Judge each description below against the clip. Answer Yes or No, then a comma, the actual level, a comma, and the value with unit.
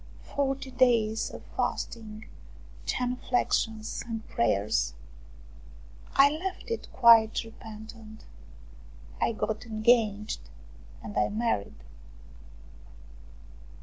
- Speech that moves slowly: Yes, slow, 80 wpm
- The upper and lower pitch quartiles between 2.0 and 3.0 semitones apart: Yes, narrow, 2.4 semitones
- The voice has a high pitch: Yes, high, 225 Hz